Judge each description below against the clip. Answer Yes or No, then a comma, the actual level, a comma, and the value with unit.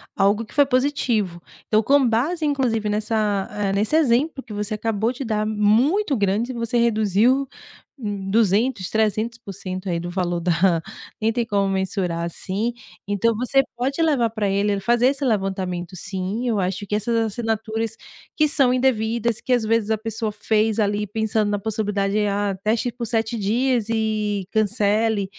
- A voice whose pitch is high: Yes, high, 215 Hz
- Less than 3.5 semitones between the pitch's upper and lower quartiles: Yes, average, 2.8 semitones